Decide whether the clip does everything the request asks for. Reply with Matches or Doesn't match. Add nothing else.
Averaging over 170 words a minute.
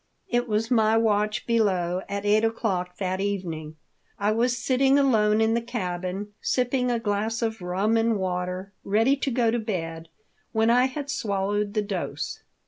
Doesn't match